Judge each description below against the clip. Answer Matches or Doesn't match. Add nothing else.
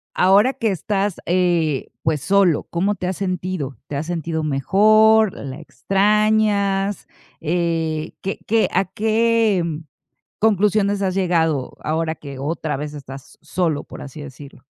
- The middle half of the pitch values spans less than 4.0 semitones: Doesn't match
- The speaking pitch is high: Doesn't match